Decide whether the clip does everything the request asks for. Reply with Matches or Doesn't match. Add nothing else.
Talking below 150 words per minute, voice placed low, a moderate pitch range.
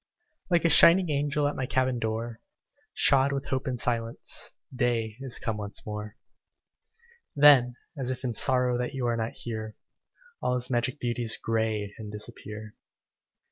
Doesn't match